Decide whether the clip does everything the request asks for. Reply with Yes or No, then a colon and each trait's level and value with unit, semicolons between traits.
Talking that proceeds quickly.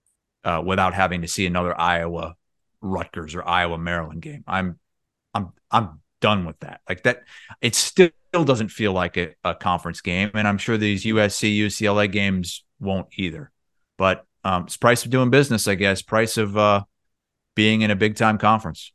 No: average, 180 wpm